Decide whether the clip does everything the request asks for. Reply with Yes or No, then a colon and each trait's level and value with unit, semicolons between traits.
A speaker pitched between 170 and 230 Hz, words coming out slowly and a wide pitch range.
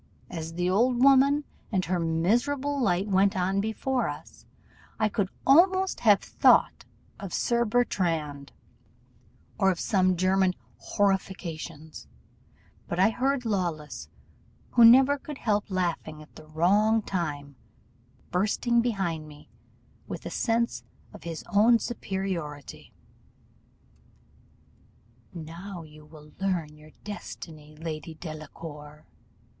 Yes: medium, 185 Hz; slow, 115 wpm; wide, 5.8 semitones